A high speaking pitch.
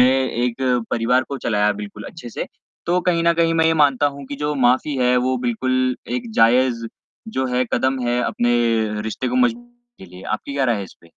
No: low, 130 Hz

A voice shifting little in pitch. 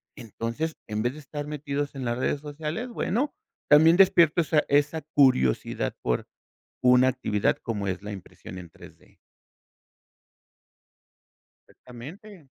No: average, 5.2 semitones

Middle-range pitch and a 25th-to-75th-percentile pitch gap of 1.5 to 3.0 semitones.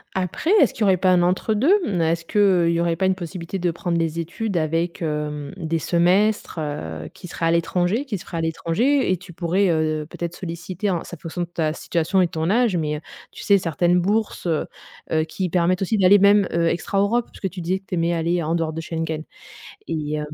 Yes: medium, 175 Hz; average, 2.7 semitones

